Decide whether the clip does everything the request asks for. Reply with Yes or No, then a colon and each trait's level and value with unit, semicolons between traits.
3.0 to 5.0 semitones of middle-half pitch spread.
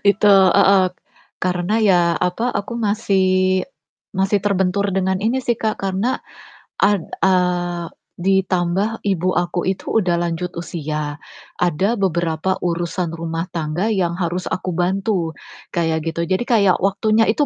No: narrow, 2.4 semitones